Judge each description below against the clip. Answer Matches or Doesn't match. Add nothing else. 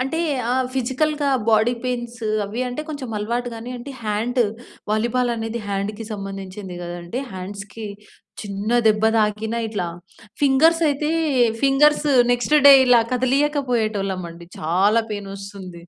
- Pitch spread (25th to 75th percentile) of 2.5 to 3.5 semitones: Doesn't match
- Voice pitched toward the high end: Matches